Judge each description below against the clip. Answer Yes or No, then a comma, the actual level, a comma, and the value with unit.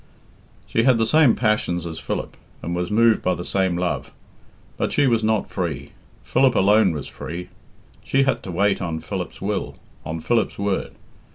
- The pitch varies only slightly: No, average, 4.5 semitones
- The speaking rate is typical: Yes, average, 175 wpm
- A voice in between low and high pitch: No, low, 100 Hz